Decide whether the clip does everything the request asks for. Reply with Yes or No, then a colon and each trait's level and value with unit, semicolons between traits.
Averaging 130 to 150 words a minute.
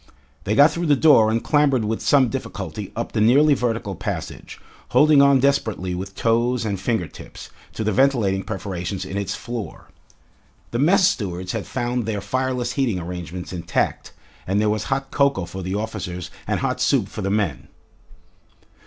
No: average, 170 wpm